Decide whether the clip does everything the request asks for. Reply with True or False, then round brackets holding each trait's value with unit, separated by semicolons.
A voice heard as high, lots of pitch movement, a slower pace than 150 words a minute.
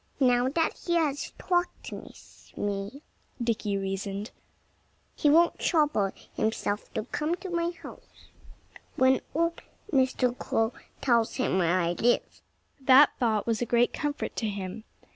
True (245 Hz; 6.2 semitones; 140 wpm)